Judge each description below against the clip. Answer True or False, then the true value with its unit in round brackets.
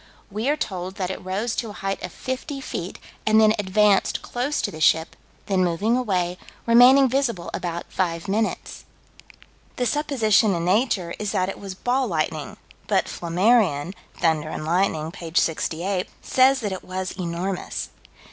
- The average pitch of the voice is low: False (195 Hz)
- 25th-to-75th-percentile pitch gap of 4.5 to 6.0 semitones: True (5.0 semitones)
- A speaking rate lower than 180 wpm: True (160 wpm)